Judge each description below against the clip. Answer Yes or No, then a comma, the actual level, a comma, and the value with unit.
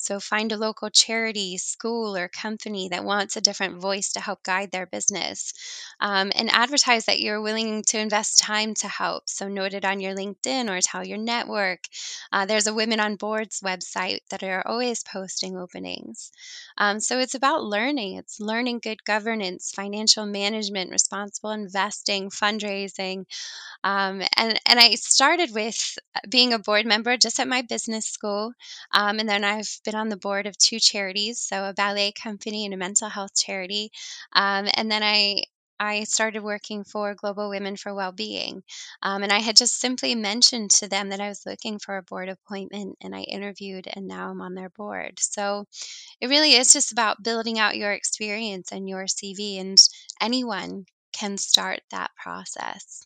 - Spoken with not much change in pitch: Yes, narrow, 2.0 semitones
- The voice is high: Yes, high, 205 Hz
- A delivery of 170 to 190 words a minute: Yes, average, 180 wpm